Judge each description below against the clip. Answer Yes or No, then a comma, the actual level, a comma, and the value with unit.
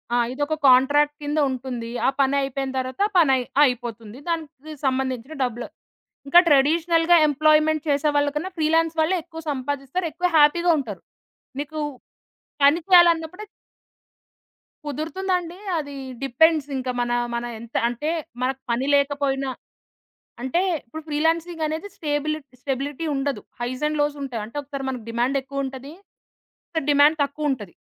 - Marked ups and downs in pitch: No, average, 3.2 semitones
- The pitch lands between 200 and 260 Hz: No, very high, 285 Hz